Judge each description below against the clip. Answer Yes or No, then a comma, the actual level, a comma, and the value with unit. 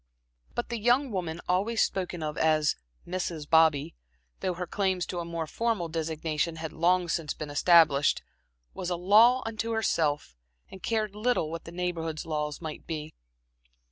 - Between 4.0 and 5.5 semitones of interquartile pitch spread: No, average, 3.5 semitones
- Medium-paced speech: Yes, average, 160 wpm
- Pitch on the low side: No, medium, 170 Hz